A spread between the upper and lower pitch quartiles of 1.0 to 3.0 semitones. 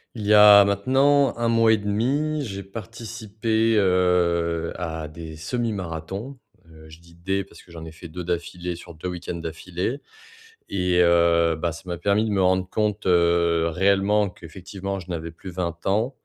No: average, 3.7 semitones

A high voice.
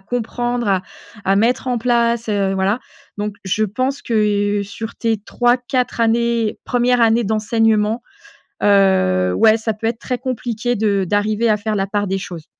Yes: high, 220 Hz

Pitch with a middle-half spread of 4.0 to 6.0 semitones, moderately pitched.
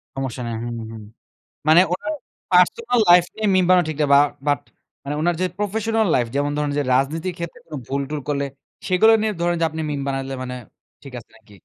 Yes: average, 4.8 semitones; medium, 155 Hz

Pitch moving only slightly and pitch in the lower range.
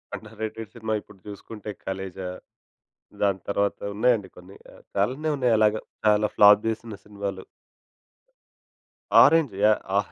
Yes: narrow, 2.1 semitones; low, 105 Hz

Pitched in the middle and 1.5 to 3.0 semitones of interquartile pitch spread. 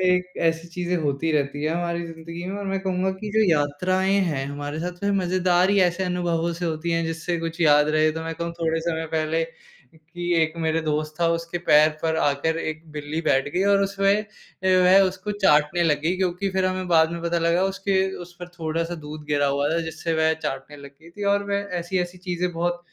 Yes: medium, 170 Hz; narrow, 2.4 semitones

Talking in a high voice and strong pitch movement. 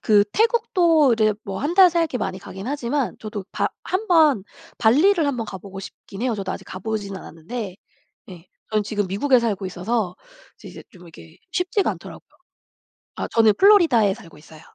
Yes: high, 220 Hz; wide, 7.3 semitones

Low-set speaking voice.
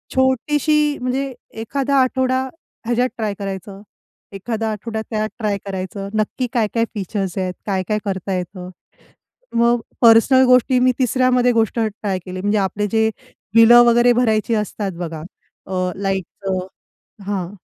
No: high, 220 Hz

